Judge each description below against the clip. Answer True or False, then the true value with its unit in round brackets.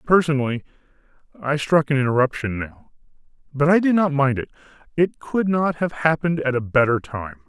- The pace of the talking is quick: False (170 wpm)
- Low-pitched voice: False (145 Hz)